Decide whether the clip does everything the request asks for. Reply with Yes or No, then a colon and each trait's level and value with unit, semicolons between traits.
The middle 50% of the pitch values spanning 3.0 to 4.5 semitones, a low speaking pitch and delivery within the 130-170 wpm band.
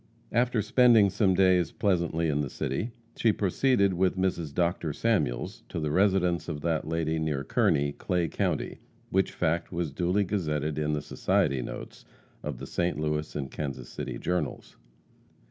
Yes: average, 4.0 semitones; very low, 85 Hz; average, 160 wpm